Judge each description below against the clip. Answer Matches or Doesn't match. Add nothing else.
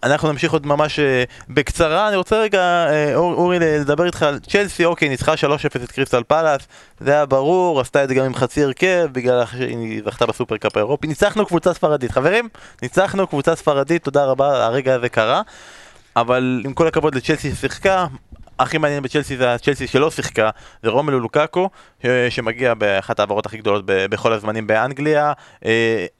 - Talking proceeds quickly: Matches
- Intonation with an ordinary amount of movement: Matches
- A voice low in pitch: Doesn't match